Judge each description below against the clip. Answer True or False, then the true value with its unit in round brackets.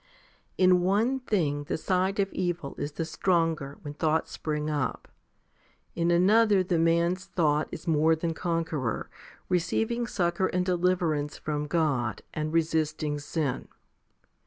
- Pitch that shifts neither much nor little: True (3.1 semitones)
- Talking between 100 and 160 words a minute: True (135 wpm)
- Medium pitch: True (165 Hz)